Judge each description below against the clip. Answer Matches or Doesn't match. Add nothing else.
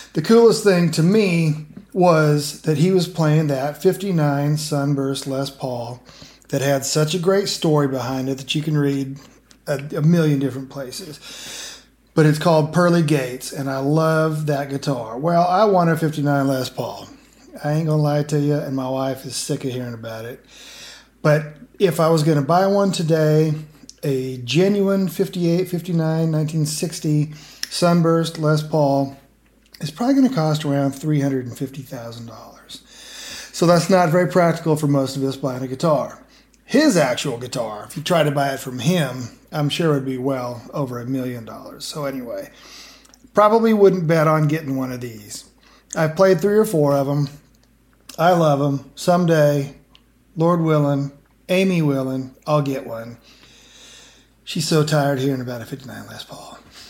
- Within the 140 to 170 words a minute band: Matches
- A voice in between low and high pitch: Matches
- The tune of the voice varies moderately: Matches